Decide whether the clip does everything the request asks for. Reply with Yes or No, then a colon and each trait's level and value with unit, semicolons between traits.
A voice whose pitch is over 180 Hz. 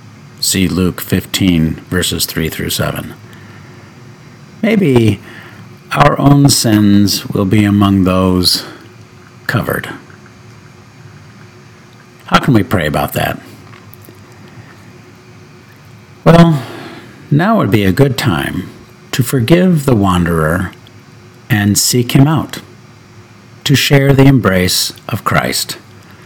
No: low, 120 Hz